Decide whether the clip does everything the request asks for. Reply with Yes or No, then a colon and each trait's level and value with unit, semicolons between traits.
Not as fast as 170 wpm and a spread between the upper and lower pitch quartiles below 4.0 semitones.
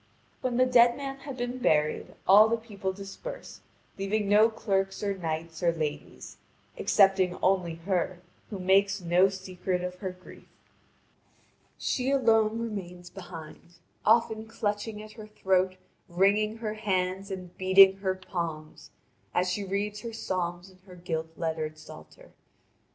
Yes: average, 140 wpm; average, 3.1 semitones